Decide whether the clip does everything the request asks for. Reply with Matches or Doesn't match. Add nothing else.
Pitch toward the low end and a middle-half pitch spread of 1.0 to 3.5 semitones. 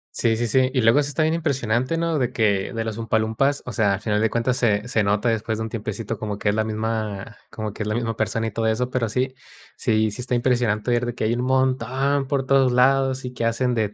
Matches